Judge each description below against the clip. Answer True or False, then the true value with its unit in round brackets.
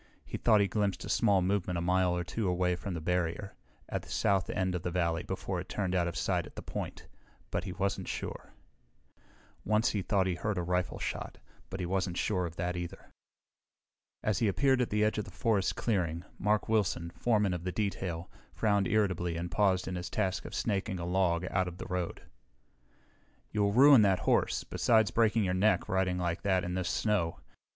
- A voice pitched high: False (95 Hz)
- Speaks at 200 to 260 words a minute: True (205 wpm)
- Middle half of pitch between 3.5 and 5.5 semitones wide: False (2.7 semitones)